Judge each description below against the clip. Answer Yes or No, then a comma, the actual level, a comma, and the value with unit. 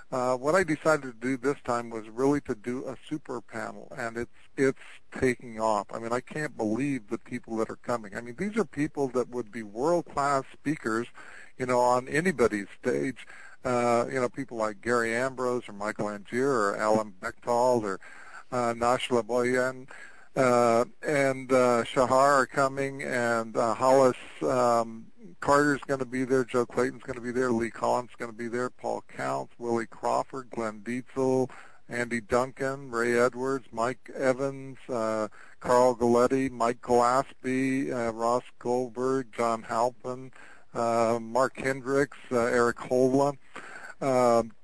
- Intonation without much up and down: Yes, narrow, 2.3 semitones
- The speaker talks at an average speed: Yes, average, 160 wpm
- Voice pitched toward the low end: Yes, low, 125 Hz